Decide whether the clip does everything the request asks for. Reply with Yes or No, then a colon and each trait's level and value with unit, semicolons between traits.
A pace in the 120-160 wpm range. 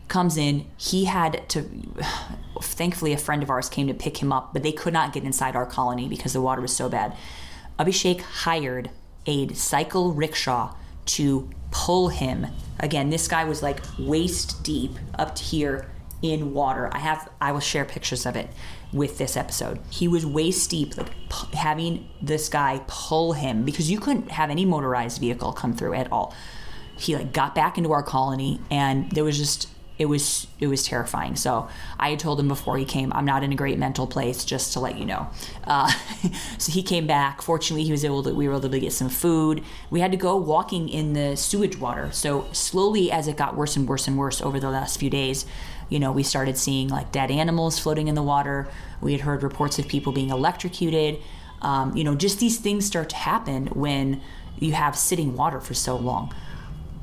No: fast, 205 wpm